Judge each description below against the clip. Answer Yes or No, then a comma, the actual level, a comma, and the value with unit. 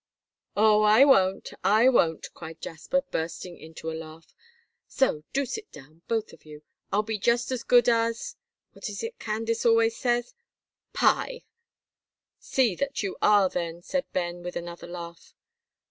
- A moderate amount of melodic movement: No, wide, 5.9 semitones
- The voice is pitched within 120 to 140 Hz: No, high, 210 Hz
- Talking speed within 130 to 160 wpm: Yes, average, 155 wpm